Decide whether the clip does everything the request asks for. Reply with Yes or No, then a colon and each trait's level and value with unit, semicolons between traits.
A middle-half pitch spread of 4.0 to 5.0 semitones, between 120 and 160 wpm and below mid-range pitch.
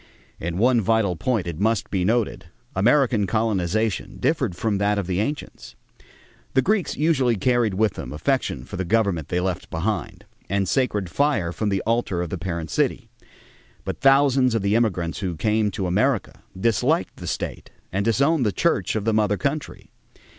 No: average, 4.7 semitones; average, 175 wpm; low, 105 Hz